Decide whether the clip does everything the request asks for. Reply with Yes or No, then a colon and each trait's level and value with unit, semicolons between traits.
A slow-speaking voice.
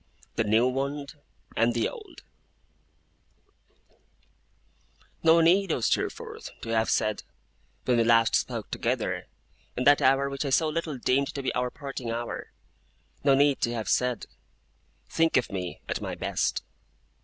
No: average, 145 wpm